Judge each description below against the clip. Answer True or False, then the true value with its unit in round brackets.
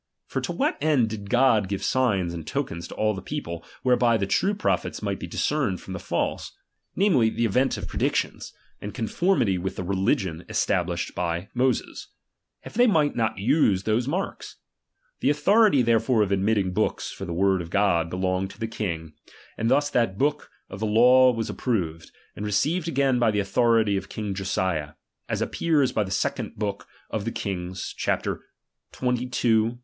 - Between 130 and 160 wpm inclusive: False (180 wpm)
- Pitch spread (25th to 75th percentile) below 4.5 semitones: False (5.0 semitones)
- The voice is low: True (110 Hz)